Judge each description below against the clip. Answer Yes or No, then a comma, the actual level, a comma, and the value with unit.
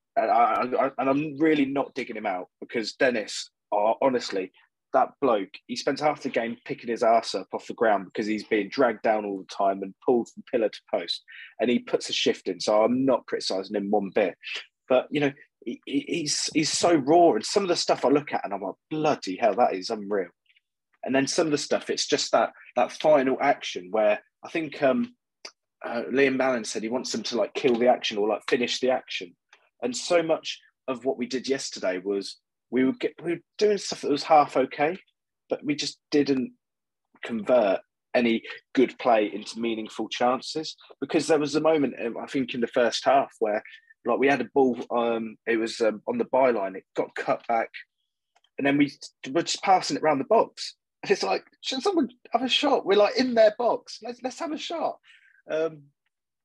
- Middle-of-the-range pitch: Yes, medium, 145 Hz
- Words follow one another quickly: Yes, fast, 210 wpm